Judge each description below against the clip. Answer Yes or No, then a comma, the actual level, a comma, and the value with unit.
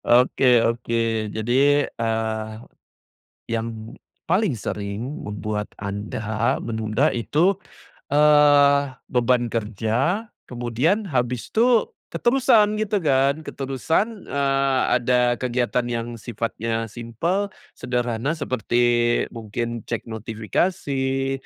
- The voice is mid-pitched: No, low, 120 Hz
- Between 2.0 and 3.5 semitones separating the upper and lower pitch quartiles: No, average, 3.9 semitones